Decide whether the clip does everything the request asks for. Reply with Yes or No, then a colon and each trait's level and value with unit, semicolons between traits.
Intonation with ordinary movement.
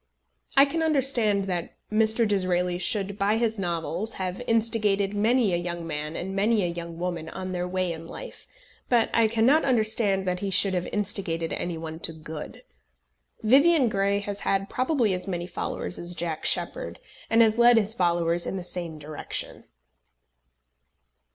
Yes: average, 4.3 semitones